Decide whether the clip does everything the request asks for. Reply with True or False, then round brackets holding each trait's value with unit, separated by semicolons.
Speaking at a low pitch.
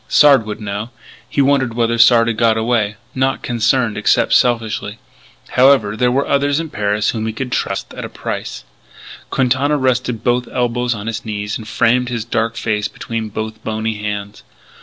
True (115 Hz)